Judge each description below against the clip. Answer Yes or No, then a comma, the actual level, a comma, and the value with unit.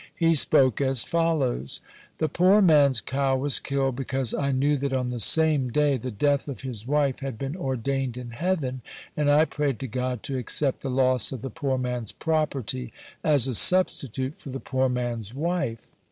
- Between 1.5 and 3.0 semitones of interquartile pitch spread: Yes, narrow, 2.6 semitones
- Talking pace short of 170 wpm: No, average, 185 wpm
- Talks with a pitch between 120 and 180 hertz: Yes, low, 135 Hz